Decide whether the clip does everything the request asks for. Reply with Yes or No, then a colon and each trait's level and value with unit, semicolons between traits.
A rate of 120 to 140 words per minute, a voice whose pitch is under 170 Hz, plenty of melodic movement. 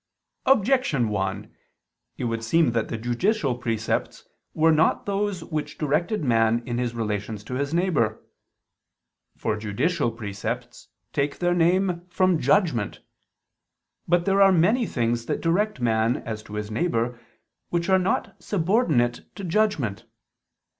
Yes: slow, 135 wpm; medium, 140 Hz; wide, 7.7 semitones